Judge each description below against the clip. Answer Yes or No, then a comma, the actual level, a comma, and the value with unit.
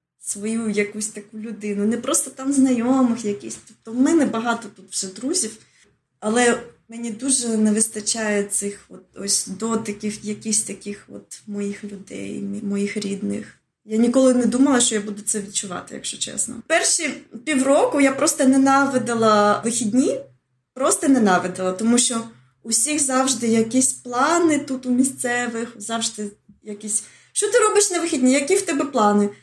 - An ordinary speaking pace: Yes, average, 145 wpm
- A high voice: Yes, high, 230 Hz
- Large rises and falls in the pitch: No, average, 4.1 semitones